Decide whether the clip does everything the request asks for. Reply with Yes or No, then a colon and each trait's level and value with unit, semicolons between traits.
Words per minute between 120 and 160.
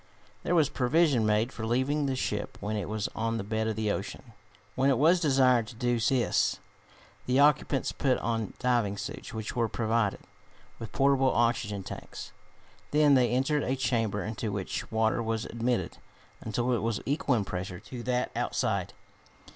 No: average, 170 wpm